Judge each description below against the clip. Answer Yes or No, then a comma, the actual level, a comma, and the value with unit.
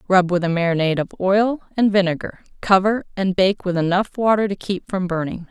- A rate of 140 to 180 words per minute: No, average, 195 wpm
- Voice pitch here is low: No, high, 190 Hz